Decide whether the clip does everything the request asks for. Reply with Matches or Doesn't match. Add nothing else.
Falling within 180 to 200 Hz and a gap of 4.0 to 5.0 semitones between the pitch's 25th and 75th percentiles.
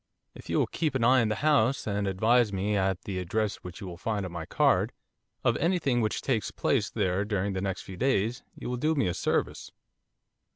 Doesn't match